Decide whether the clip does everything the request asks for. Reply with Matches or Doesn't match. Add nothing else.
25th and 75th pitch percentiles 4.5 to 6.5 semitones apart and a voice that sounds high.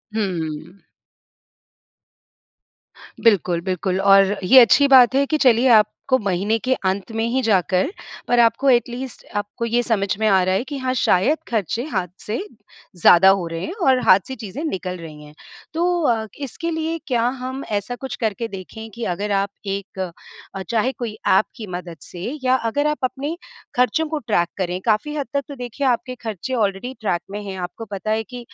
Matches